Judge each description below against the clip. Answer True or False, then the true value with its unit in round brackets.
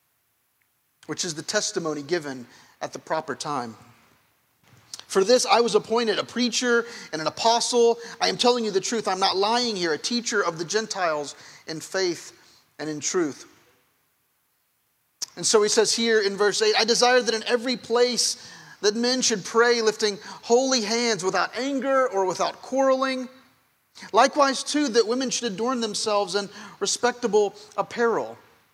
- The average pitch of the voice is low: False (225 Hz)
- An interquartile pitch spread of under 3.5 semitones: False (4.0 semitones)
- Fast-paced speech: False (155 wpm)